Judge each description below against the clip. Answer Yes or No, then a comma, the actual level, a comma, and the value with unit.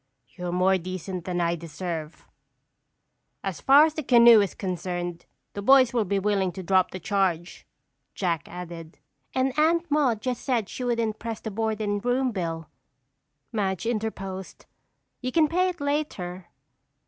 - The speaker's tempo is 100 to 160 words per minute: Yes, average, 155 wpm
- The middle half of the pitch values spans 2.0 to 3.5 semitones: No, wide, 5.5 semitones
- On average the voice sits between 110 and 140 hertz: No, high, 200 Hz